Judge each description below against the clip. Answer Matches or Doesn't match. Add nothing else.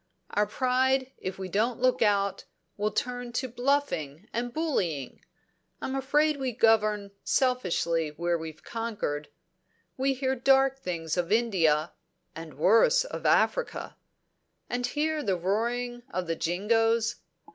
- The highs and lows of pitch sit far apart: Matches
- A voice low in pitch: Doesn't match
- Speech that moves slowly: Matches